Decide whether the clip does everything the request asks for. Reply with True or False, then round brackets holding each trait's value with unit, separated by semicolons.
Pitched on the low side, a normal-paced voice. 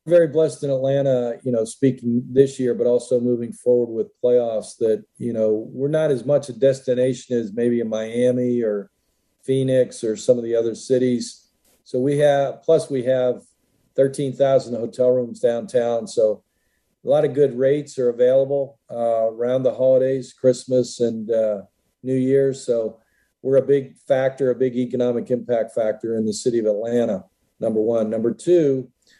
True (125 Hz; 170 wpm)